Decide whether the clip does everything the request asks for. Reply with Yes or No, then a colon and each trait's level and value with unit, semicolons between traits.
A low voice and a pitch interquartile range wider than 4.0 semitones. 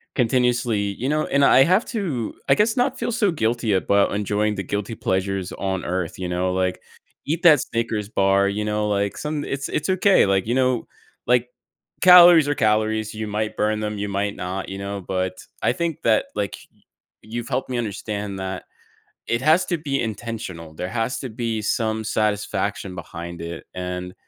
Yes: low, 110 Hz; average, 4.6 semitones